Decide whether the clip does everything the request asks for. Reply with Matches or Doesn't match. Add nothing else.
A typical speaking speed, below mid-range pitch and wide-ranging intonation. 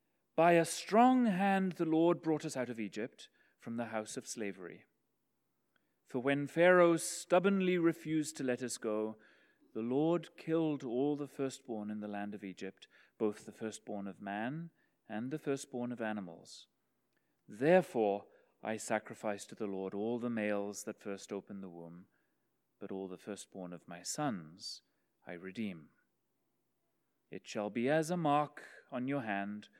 Matches